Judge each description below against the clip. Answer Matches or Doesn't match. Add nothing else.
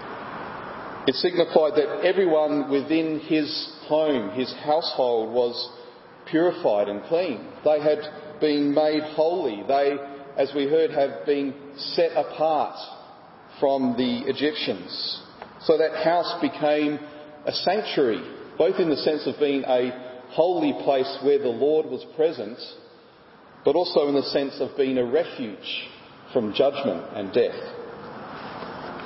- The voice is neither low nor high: Matches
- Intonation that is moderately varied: Doesn't match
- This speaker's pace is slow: Matches